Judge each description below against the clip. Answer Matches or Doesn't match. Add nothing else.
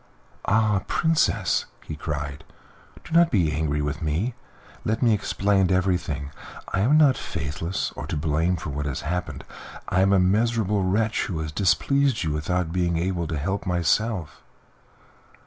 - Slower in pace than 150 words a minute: Doesn't match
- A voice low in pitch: Matches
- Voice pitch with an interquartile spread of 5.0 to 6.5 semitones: Matches